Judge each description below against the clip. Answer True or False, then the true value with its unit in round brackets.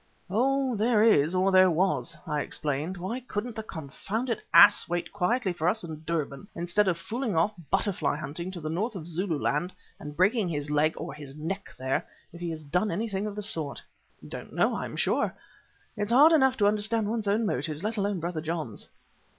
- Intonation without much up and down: False (5.1 semitones)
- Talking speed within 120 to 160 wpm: False (195 wpm)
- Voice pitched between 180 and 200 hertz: True (185 Hz)